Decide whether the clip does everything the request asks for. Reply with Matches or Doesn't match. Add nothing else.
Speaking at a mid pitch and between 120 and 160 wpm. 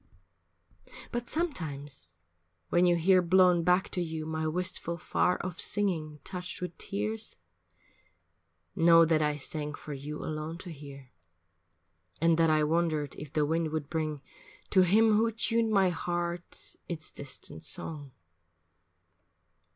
Matches